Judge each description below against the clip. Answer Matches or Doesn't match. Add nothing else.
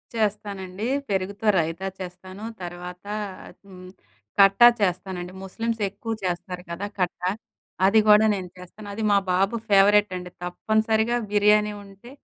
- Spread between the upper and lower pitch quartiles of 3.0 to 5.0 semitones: Doesn't match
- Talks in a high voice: Matches